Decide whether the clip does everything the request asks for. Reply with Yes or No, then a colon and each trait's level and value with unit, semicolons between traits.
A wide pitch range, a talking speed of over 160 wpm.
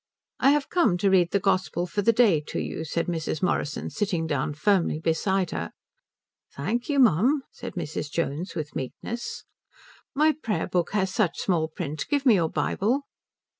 Yes: wide, 5.8 semitones; average, 170 wpm